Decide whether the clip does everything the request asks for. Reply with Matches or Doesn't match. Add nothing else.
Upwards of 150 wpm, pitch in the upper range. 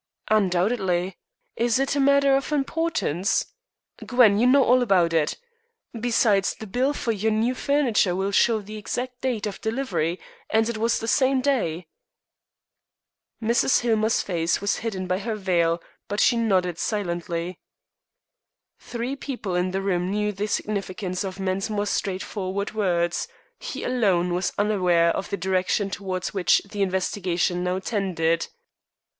Doesn't match